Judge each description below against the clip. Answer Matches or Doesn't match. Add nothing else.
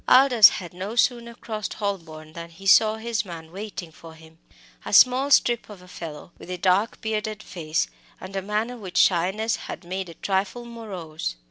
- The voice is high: Matches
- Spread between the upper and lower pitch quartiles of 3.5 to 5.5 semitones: Matches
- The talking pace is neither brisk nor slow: Matches